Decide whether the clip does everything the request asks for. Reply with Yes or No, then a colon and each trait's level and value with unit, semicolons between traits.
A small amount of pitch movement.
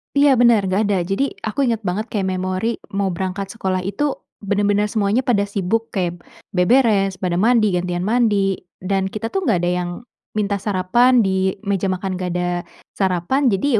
No: average, 3.4 semitones